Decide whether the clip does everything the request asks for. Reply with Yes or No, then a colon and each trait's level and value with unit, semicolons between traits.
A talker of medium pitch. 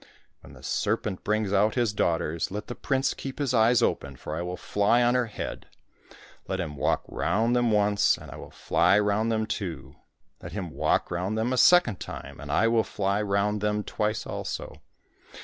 No: low, 105 Hz